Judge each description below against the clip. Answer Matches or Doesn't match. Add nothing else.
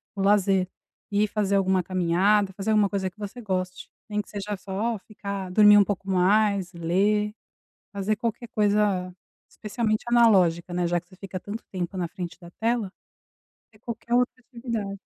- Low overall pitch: Doesn't match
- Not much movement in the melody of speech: Matches